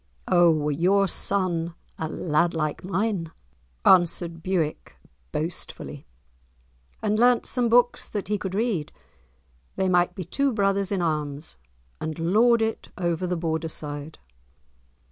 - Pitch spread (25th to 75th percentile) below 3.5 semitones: No, average, 3.8 semitones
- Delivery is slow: Yes, slow, 125 wpm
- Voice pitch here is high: No, medium, 175 Hz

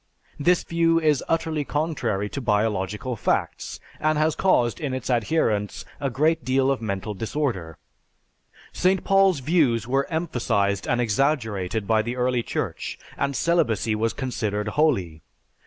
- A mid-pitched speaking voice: No, low, 125 Hz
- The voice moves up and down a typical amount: No, wide, 6.2 semitones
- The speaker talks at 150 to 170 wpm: No, average, 140 wpm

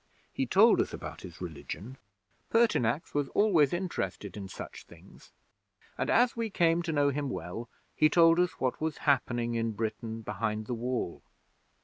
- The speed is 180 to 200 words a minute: No, average, 160 wpm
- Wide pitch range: Yes, wide, 7.0 semitones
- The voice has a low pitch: Yes, low, 130 Hz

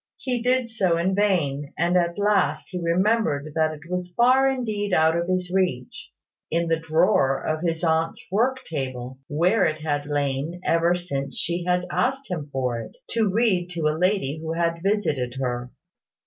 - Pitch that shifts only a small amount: No, average, 4.5 semitones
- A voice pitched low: No, medium, 170 Hz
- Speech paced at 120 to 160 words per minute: No, average, 175 wpm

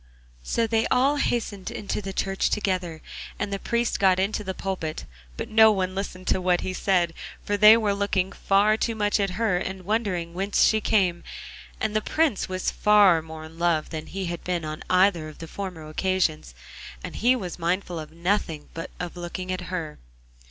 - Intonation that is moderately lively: Yes, average, 3.1 semitones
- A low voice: No, medium, 185 Hz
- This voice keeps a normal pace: Yes, average, 195 wpm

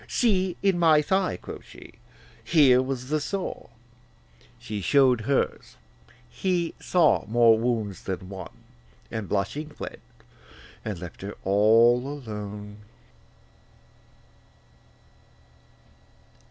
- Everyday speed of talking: No, slow, 100 wpm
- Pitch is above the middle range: No, low, 125 Hz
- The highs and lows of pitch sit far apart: Yes, wide, 6.8 semitones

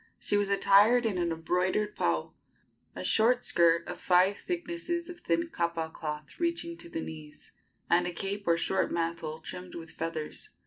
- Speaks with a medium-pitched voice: Yes, medium, 180 Hz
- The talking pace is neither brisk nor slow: Yes, average, 170 wpm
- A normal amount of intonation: No, wide, 6.3 semitones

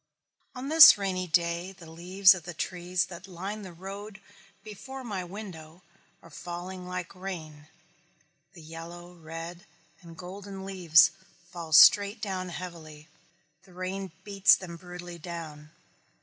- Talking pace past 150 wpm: No, slow, 135 wpm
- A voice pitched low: No, medium, 180 Hz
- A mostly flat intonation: Yes, narrow, 2.3 semitones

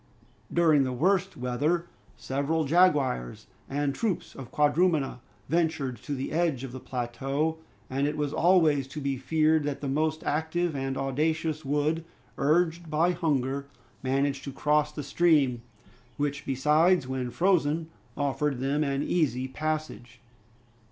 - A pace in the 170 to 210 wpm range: No, average, 140 wpm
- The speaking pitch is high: No, medium, 145 Hz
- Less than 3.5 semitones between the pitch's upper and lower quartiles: Yes, average, 3.0 semitones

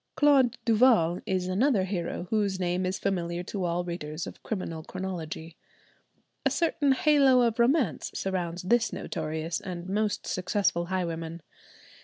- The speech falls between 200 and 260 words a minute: No, slow, 135 wpm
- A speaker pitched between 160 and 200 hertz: Yes, medium, 185 Hz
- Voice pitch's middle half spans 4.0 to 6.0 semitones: Yes, average, 4.5 semitones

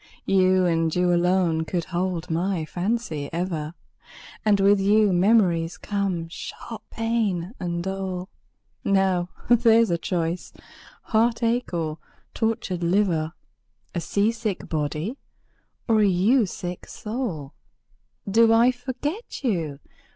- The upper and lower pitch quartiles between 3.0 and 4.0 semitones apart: No, average, 4.5 semitones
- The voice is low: No, medium, 185 Hz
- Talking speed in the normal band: No, slow, 115 wpm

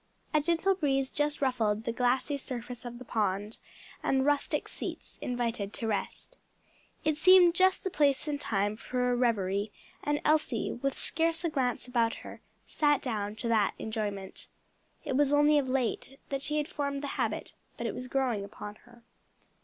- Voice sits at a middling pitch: No, very high, 255 Hz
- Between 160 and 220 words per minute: Yes, average, 175 wpm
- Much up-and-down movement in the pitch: No, average, 4.5 semitones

